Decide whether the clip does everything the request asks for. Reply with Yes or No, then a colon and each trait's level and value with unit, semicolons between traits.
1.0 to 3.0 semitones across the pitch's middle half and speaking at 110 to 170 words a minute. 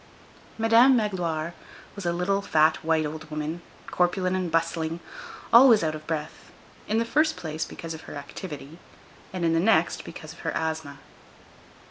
No: average, 3.6 semitones; average, 155 wpm